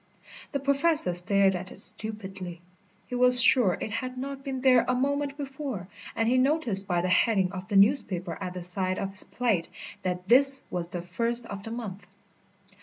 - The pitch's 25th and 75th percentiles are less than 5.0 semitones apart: No, wide, 5.6 semitones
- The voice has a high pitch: Yes, high, 215 Hz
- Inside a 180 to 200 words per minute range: Yes, average, 185 wpm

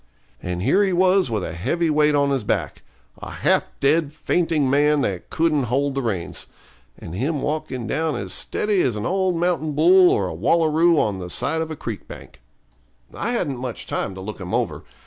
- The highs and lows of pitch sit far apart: Yes, wide, 6.7 semitones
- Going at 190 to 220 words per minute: Yes, average, 200 wpm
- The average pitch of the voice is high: No, medium, 145 Hz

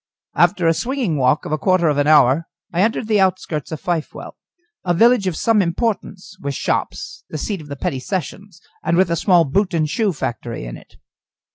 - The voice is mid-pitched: Yes, medium, 170 Hz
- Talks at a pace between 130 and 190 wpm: No, fast, 205 wpm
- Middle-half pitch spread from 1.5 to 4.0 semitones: No, average, 4.5 semitones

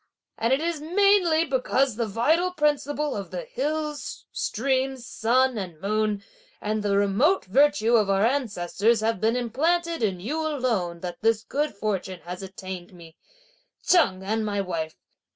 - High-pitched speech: Yes, high, 230 Hz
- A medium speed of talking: Yes, average, 150 wpm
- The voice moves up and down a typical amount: No, wide, 6.9 semitones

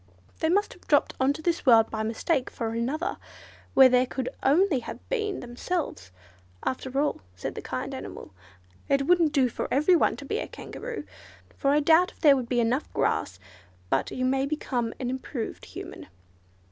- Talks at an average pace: Yes, average, 185 wpm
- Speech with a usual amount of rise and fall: Yes, average, 4.6 semitones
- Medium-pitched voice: No, very high, 270 Hz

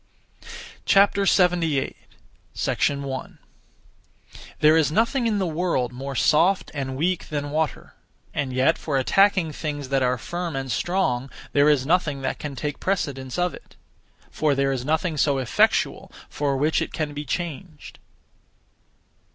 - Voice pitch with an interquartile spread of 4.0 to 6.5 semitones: Yes, average, 4.3 semitones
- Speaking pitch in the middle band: Yes, medium, 150 Hz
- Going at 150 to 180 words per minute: No, average, 140 wpm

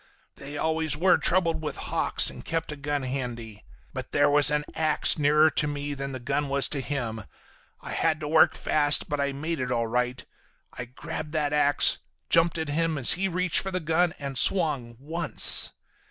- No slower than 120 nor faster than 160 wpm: No, average, 190 wpm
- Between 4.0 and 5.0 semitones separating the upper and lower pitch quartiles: No, average, 2.7 semitones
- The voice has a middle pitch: Yes, medium, 145 Hz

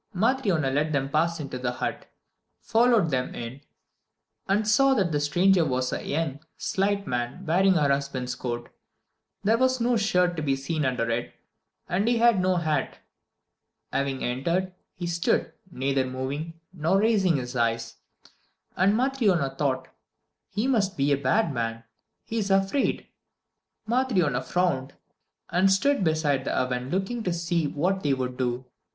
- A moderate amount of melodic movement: No, wide, 6.5 semitones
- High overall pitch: No, medium, 165 Hz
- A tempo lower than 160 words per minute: Yes, average, 150 wpm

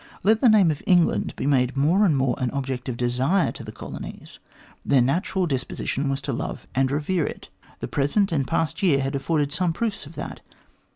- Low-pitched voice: No, medium, 145 Hz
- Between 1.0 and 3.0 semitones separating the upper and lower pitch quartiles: No, average, 4.8 semitones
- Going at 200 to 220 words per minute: Yes, fast, 205 wpm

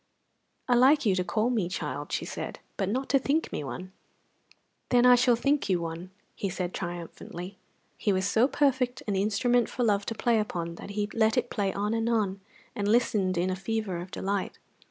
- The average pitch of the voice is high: Yes, high, 205 Hz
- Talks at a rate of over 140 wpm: Yes, average, 200 wpm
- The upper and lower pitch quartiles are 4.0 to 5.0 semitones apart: Yes, average, 4.6 semitones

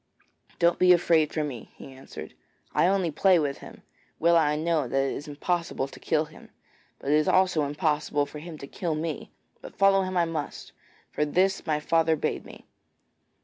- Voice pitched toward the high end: No, medium, 155 Hz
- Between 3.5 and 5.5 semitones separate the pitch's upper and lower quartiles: No, average, 2.7 semitones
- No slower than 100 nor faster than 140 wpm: No, average, 190 wpm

